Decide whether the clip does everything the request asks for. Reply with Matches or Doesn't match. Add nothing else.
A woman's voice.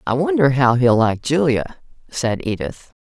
Matches